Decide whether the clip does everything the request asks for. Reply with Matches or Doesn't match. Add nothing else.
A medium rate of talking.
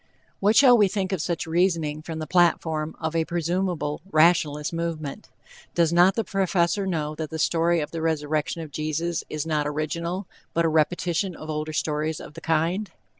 Matches